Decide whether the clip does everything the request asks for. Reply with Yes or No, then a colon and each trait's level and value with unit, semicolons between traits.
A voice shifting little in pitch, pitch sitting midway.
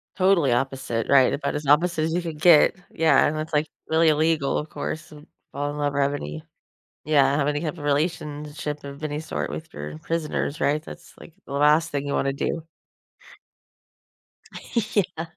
Yes: narrow, 2.1 semitones; medium, 150 Hz